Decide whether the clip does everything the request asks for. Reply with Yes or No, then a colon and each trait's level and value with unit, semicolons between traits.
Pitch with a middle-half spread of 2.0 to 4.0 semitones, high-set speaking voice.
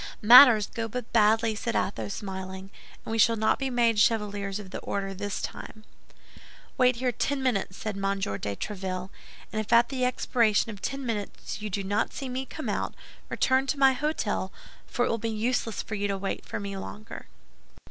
Yes: average, 3.5 semitones; high, 215 Hz